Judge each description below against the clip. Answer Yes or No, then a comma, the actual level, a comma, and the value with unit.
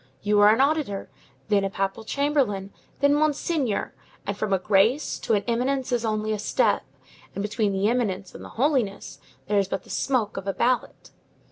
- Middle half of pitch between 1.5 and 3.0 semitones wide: No, average, 4.6 semitones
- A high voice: Yes, high, 215 Hz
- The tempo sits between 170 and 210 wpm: Yes, average, 190 wpm